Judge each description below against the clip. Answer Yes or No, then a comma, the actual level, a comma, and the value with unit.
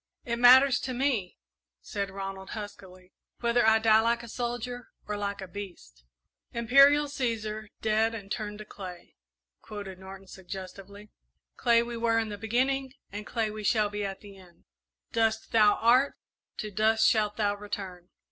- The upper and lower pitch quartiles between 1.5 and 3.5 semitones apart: Yes, average, 2.9 semitones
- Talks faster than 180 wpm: No, average, 160 wpm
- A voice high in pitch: Yes, high, 215 Hz